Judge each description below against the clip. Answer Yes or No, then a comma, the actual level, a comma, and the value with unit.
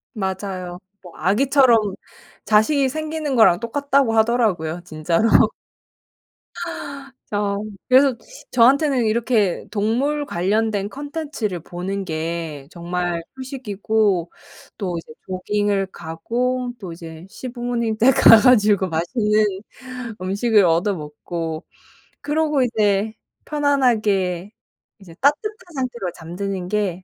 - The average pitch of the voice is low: No, high, 210 Hz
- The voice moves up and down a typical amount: No, wide, 5.8 semitones